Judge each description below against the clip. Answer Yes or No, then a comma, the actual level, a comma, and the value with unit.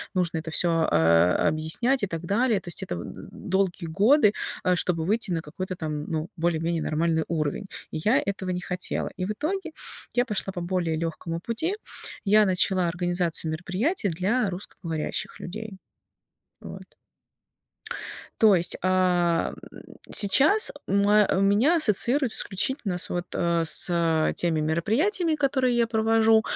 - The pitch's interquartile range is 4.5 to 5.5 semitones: Yes, average, 4.8 semitones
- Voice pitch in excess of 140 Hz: Yes, medium, 185 Hz